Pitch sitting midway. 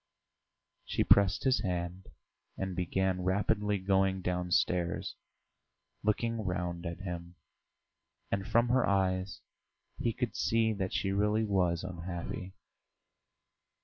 No: very low, 95 Hz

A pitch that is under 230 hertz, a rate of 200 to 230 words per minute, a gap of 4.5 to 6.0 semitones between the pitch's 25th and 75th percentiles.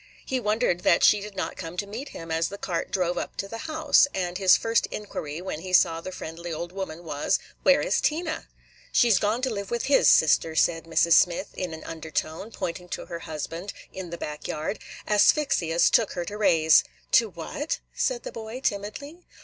Yes: medium, 185 Hz; fast, 205 wpm; average, 5.1 semitones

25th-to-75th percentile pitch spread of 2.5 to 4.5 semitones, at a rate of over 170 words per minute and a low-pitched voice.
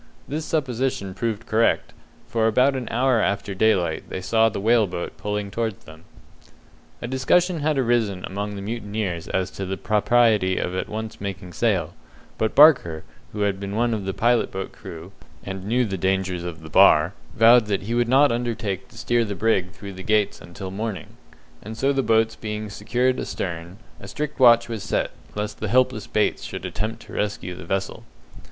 Yes: average, 3.6 semitones; average, 185 wpm; low, 105 Hz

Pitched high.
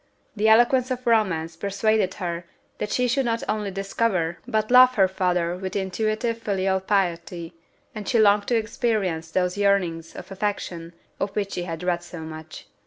Yes: high, 195 Hz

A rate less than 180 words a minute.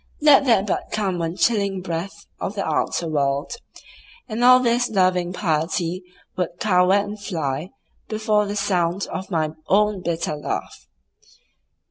Yes: average, 140 wpm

